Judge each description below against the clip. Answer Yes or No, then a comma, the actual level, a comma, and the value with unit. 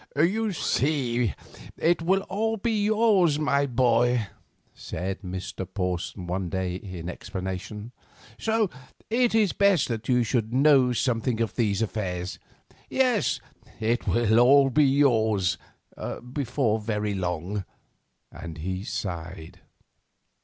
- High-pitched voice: No, low, 115 Hz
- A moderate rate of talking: No, slow, 115 wpm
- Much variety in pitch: Yes, wide, 7.8 semitones